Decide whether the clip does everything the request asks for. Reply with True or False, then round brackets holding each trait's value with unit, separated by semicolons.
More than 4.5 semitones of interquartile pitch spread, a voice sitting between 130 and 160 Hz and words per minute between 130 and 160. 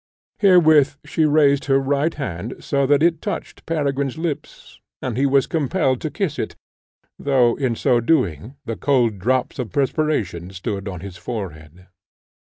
True (5.2 semitones; 135 Hz; 155 wpm)